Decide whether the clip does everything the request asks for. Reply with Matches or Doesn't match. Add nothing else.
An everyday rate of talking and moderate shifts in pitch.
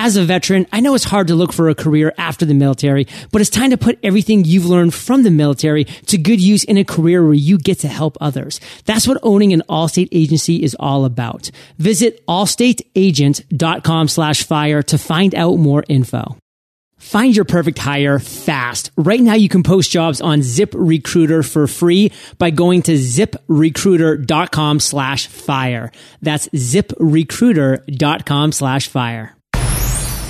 Matches